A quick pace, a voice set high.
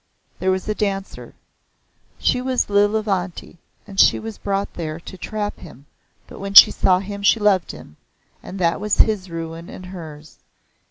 No: average, 165 wpm; high, 195 Hz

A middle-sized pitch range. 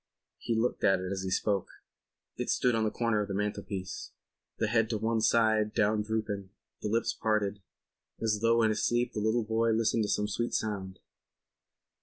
No: narrow, 1.6 semitones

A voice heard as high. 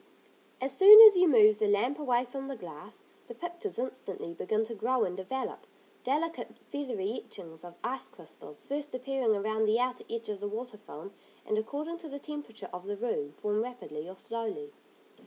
Yes: high, 230 Hz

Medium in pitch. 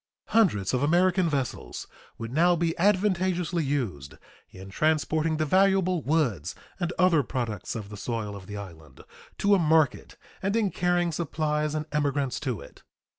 Yes: medium, 155 Hz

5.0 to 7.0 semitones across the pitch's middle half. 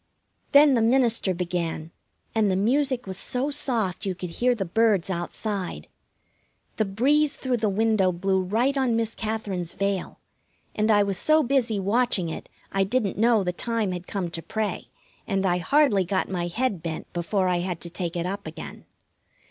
No: average, 4.4 semitones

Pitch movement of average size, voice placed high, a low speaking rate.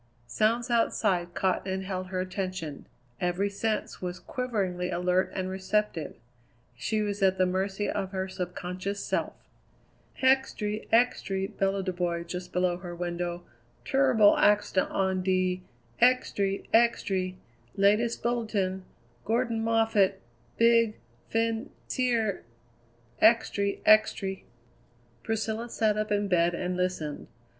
Yes: average, 3.2 semitones; high, 195 Hz; slow, 115 wpm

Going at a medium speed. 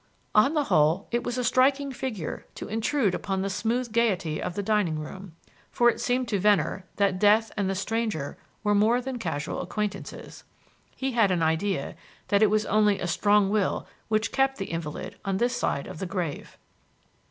Yes: average, 185 wpm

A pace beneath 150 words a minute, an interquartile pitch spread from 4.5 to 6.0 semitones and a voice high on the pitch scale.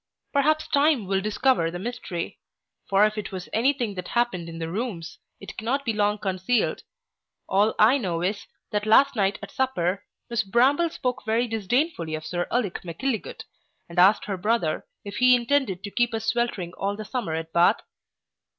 No: average, 180 wpm; average, 4.8 semitones; high, 215 Hz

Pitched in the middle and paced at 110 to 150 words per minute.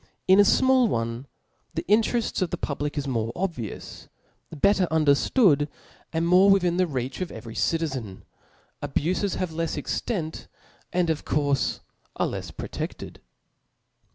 Yes: medium, 165 Hz; average, 140 wpm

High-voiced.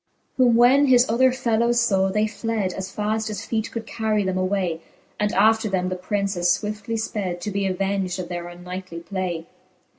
Yes: high, 200 Hz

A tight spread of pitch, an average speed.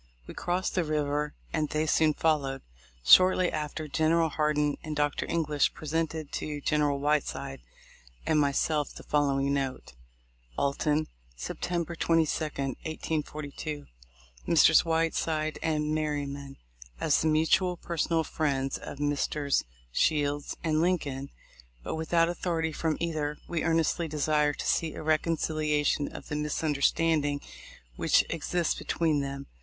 No: narrow, 1.9 semitones; slow, 130 wpm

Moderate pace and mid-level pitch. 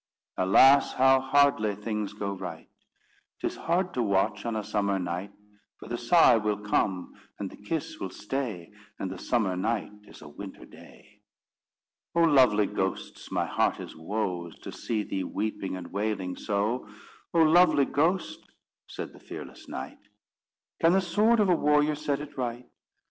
No: average, 160 wpm; low, 110 Hz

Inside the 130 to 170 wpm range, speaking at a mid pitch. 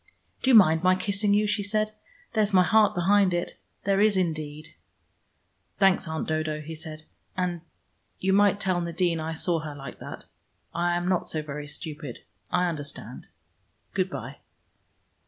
Yes: average, 165 wpm; medium, 175 Hz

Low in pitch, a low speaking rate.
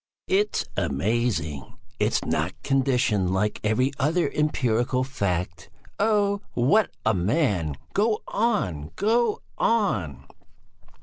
Yes: low, 125 Hz; slow, 105 wpm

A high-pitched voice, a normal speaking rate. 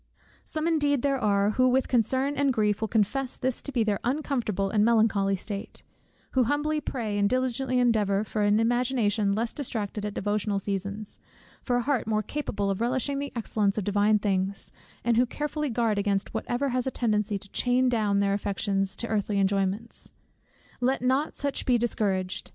Yes: high, 220 Hz; average, 180 wpm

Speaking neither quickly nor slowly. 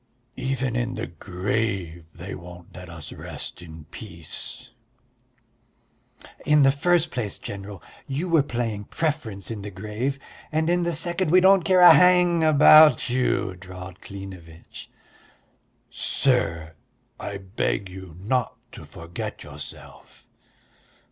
No: slow, 125 wpm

